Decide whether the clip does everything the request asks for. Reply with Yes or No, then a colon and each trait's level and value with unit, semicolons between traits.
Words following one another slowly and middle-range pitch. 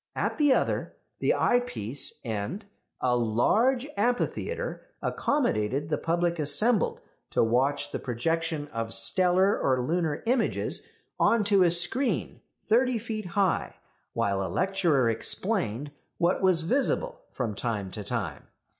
Yes: slow, 130 wpm; medium, 170 Hz